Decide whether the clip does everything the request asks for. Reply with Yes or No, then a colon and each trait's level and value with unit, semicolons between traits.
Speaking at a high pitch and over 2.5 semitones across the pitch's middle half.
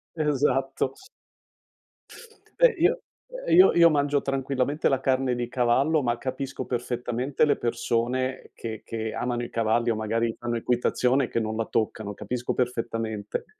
No: low, 125 Hz; average, 2.9 semitones